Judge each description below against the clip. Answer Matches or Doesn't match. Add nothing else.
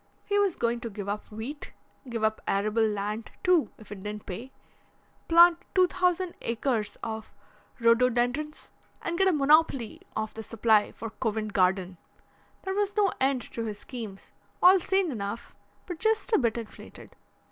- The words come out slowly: Doesn't match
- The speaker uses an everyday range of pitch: Doesn't match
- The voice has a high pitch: Matches